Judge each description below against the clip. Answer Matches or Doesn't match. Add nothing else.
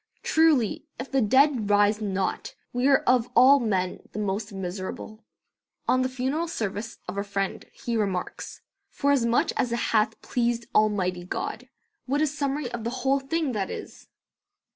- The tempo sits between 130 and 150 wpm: Doesn't match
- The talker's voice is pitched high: Matches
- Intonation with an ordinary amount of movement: Matches